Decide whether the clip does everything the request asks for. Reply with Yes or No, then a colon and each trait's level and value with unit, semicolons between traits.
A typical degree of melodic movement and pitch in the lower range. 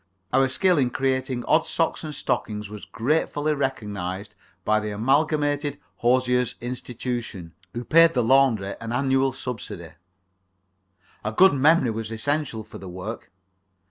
Yes: average, 4.6 semitones; low, 125 Hz